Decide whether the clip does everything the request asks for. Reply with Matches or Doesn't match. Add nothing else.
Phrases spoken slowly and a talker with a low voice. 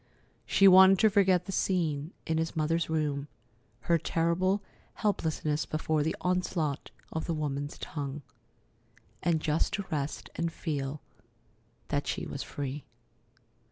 Doesn't match